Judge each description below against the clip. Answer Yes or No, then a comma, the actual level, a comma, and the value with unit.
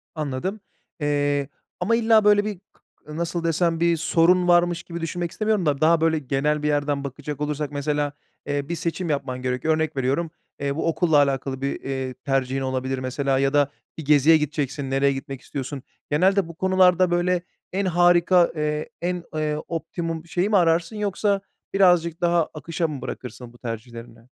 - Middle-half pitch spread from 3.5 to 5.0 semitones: Yes, average, 3.9 semitones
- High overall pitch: No, medium, 155 Hz